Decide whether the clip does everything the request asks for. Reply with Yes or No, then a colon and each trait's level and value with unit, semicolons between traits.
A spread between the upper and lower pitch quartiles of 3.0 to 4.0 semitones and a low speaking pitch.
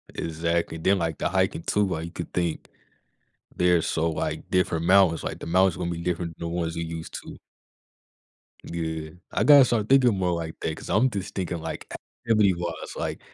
No: narrow, 2.5 semitones; very low, 85 Hz